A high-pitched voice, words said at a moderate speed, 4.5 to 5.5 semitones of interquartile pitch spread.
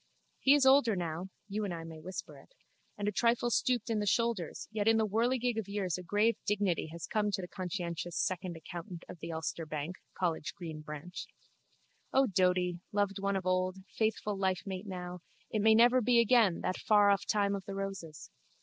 No: high, 195 Hz; average, 195 wpm; average, 3.5 semitones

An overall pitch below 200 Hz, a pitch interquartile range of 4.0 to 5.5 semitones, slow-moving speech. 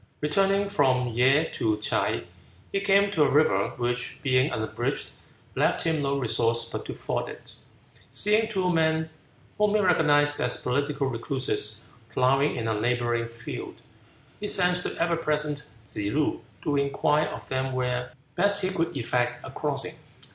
No: medium, 140 Hz; average, 5.2 semitones; average, 155 wpm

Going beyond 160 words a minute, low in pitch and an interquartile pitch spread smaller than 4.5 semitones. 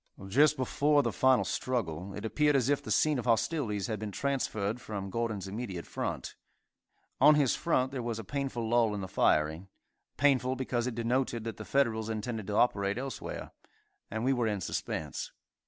Yes: average, 180 wpm; low, 115 Hz; average, 4.1 semitones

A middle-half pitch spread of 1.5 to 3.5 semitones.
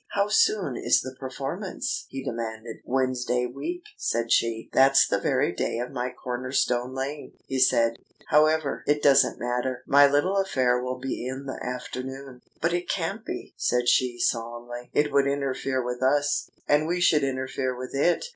Yes: average, 2.8 semitones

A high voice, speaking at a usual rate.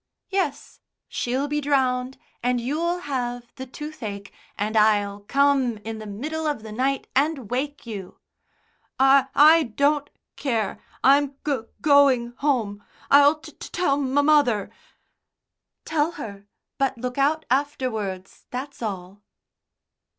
No: very high, 265 Hz; slow, 130 wpm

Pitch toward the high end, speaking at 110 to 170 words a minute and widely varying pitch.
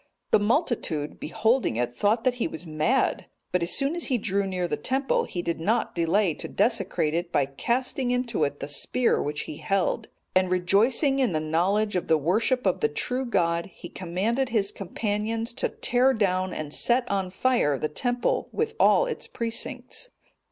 No: high, 200 Hz; average, 185 wpm; wide, 6.4 semitones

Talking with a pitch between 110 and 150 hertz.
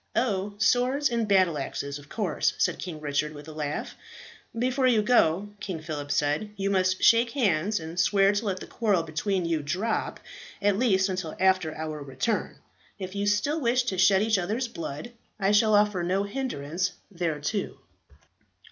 No: high, 190 Hz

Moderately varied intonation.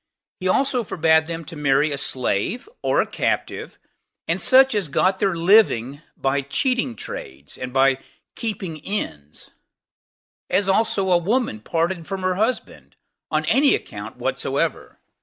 No: wide, 7.2 semitones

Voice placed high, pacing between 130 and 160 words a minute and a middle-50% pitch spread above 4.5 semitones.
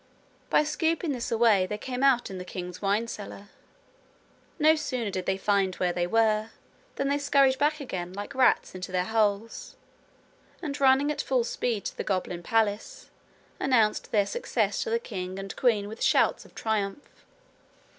No: high, 220 Hz; average, 170 wpm; wide, 5.4 semitones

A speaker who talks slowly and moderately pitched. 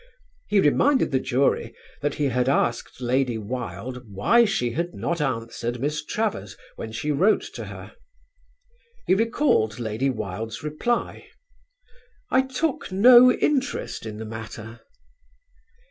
No: slow, 130 wpm; low, 130 Hz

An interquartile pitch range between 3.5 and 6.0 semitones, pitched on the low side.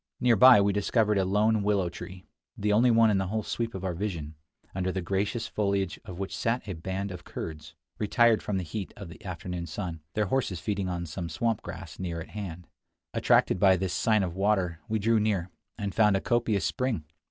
No: average, 3.1 semitones; low, 100 Hz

